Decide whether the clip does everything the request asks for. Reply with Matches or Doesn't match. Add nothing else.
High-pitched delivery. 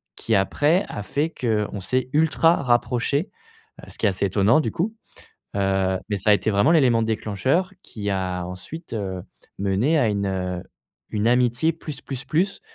Doesn't match